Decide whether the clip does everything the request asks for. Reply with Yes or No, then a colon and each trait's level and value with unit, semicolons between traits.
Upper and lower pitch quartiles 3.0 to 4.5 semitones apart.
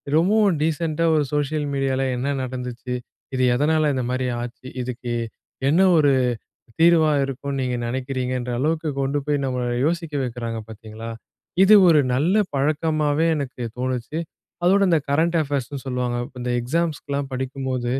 Yes: average, 3.7 semitones